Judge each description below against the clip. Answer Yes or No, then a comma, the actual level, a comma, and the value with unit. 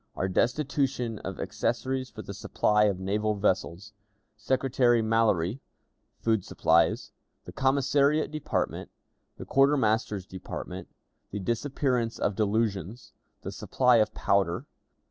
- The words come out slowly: Yes, slow, 110 wpm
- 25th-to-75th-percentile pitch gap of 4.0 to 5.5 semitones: Yes, average, 4.7 semitones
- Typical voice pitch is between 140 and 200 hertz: No, low, 115 Hz